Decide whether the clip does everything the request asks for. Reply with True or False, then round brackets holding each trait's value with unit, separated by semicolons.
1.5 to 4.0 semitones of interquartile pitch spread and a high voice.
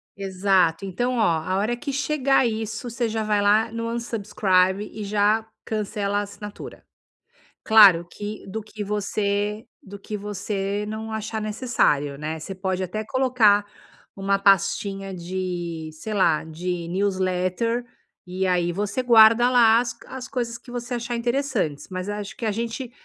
True (3.4 semitones; 205 Hz)